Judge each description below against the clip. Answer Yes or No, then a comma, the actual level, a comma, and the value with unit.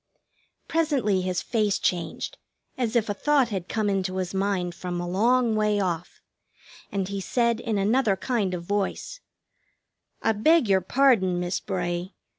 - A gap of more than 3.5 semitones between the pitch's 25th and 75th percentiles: Yes, average, 4.2 semitones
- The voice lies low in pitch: No, high, 200 Hz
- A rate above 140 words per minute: Yes, average, 155 wpm